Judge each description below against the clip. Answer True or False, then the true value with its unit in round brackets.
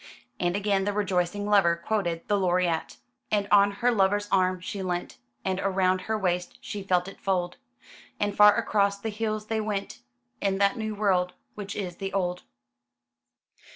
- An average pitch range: False (2.2 semitones)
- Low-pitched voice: False (195 Hz)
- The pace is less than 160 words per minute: False (165 wpm)